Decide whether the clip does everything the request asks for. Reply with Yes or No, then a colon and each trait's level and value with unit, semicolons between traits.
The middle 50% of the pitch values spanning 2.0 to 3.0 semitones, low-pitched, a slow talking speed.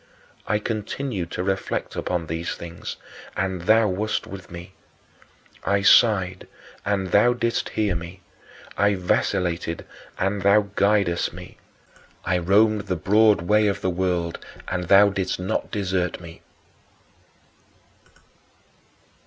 Yes: narrow, 2.6 semitones; very low, 95 Hz; slow, 120 wpm